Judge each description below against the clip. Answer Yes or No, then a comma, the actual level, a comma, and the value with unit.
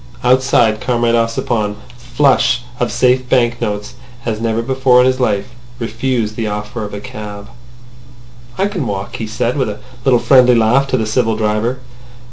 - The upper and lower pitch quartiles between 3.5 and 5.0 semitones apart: No, average, 2.8 semitones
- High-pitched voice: No, low, 120 Hz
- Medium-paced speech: Yes, average, 160 wpm